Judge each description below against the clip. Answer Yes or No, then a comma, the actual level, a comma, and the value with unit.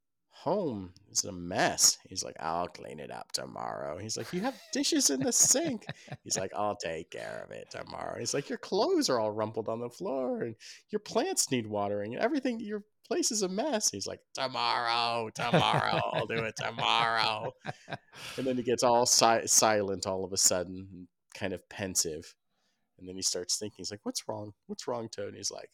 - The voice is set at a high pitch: No, low, 120 Hz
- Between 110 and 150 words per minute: No, average, 200 wpm